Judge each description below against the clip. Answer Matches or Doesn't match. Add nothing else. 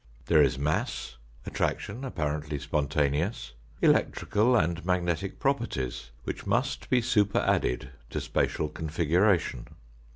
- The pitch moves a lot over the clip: Matches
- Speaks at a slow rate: Matches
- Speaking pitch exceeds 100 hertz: Doesn't match